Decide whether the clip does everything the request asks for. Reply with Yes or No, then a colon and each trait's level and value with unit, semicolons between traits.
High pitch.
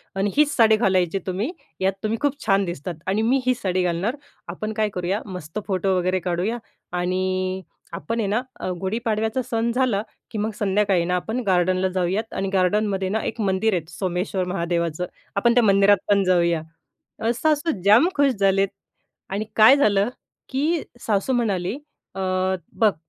Yes: high, 195 Hz